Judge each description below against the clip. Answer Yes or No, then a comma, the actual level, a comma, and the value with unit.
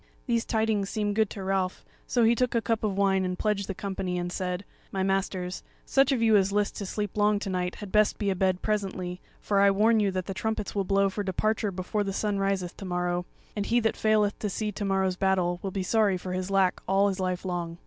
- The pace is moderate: No, fast, 240 wpm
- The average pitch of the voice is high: Yes, high, 195 Hz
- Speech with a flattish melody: Yes, narrow, 2.1 semitones